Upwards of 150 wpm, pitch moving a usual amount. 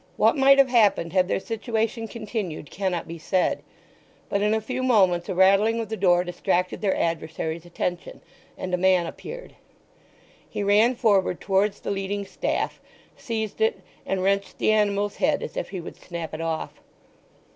Yes: average, 170 wpm; average, 3.7 semitones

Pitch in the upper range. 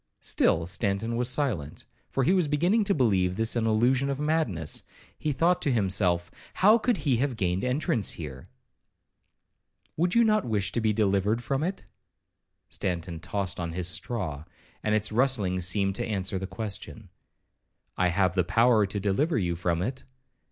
No: low, 110 Hz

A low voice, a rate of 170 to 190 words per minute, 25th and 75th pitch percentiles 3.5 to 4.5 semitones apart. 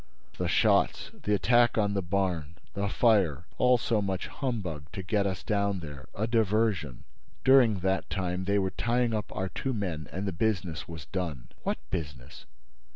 No: very low, 95 Hz; average, 155 wpm; average, 4.2 semitones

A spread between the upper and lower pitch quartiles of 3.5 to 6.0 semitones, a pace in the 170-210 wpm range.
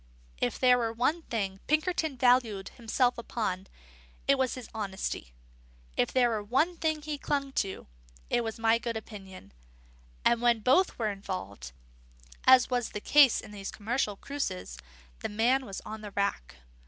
No: average, 4.2 semitones; average, 160 wpm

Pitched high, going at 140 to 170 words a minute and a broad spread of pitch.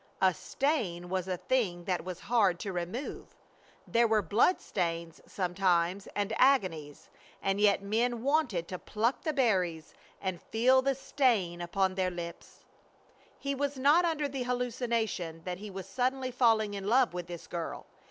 Yes: high, 205 Hz; average, 160 wpm; wide, 6.0 semitones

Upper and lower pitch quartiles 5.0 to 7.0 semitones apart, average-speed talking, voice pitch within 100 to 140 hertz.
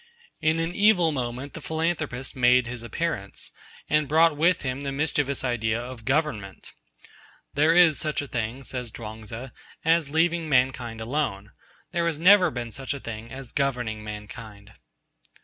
Yes: average, 5.3 semitones; average, 155 wpm; low, 135 Hz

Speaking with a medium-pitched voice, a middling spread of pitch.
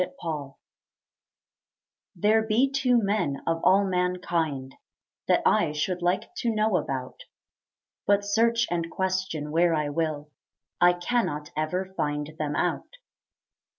Yes: medium, 175 Hz; average, 5.0 semitones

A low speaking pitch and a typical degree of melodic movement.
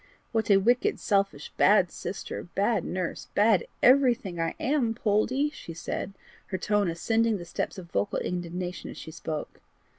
No: high, 200 Hz; average, 4.5 semitones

